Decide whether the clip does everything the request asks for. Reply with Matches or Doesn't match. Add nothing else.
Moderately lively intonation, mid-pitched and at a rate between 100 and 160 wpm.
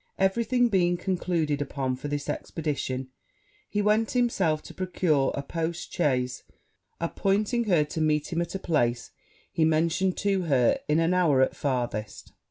Matches